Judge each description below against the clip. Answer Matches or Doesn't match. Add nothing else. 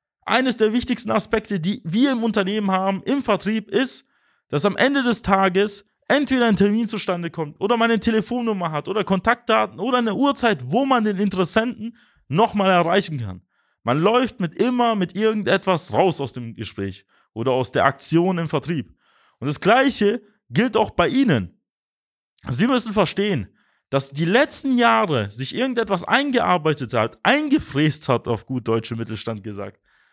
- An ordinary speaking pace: Matches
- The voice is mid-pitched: Doesn't match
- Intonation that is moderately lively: Doesn't match